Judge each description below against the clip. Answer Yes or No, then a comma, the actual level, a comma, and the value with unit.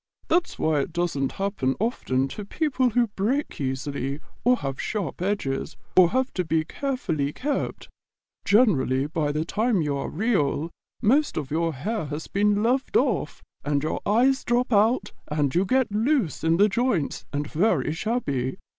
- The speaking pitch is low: No, medium, 185 Hz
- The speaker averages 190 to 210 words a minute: No, average, 165 wpm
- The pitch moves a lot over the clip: Yes, wide, 8.3 semitones